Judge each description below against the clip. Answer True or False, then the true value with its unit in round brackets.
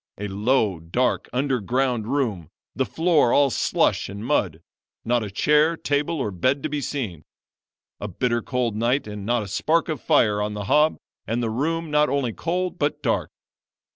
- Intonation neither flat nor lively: False (5.9 semitones)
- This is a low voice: True (125 Hz)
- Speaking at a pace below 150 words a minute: False (175 wpm)